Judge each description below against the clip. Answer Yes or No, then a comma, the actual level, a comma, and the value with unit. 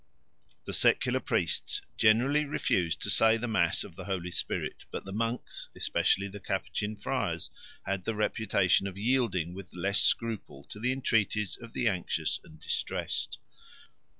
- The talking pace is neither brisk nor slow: Yes, average, 150 wpm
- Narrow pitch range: No, average, 3.3 semitones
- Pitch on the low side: Yes, low, 105 Hz